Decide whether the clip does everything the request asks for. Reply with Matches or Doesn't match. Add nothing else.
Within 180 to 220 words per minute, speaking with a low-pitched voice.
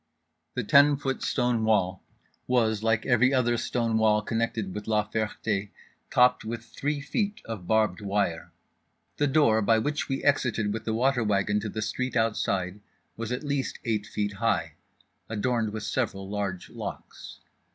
Doesn't match